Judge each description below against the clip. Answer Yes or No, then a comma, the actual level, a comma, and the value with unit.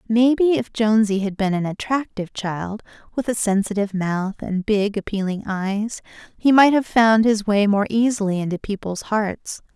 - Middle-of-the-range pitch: No, high, 210 Hz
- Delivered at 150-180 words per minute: Yes, average, 165 wpm